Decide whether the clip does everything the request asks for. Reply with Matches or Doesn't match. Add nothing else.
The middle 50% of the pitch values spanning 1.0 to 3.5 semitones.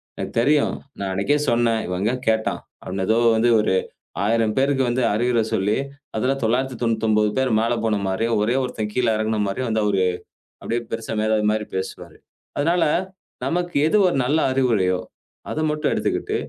Matches